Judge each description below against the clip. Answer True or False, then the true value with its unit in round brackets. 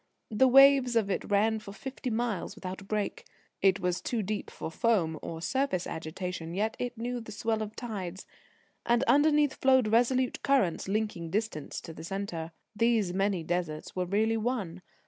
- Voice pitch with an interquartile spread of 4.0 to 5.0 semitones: True (4.7 semitones)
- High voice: True (215 Hz)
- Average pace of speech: True (170 wpm)